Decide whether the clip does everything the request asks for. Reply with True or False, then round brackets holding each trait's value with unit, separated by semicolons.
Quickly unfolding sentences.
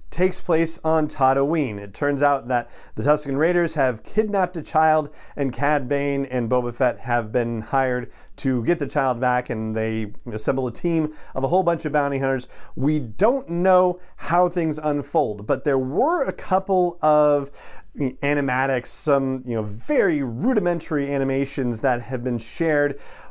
False (165 wpm)